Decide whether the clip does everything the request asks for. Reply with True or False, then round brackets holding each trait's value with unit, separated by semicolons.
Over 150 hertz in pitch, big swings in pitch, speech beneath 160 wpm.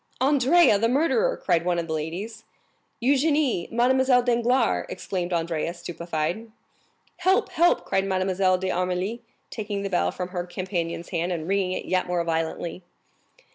True (190 Hz; 5.7 semitones; 140 wpm)